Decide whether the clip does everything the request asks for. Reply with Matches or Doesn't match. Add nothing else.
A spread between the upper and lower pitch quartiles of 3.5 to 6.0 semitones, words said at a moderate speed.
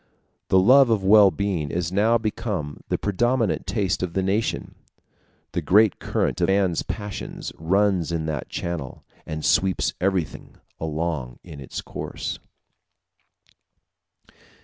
Doesn't match